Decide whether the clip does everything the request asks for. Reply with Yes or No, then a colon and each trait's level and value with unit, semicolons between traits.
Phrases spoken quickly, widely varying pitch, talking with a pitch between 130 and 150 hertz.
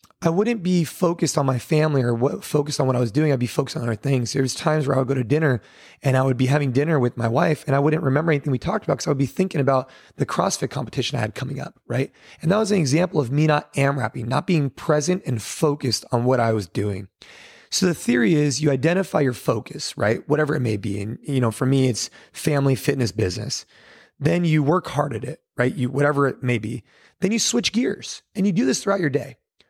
No: fast, 255 wpm; average, 3.6 semitones; medium, 140 Hz